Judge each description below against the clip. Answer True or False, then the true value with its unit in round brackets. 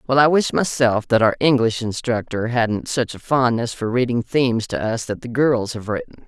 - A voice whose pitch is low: True (120 Hz)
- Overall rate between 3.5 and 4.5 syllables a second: False (4.9 syllables/s)